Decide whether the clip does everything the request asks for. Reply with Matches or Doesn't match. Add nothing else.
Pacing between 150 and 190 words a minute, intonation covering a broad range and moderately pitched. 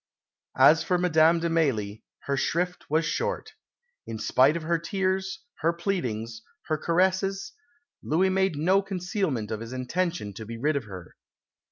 Matches